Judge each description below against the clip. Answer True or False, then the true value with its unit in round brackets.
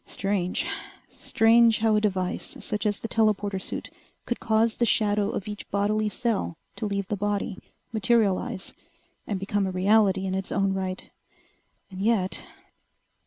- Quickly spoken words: False (150 wpm)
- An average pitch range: False (2.2 semitones)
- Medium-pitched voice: False (205 Hz)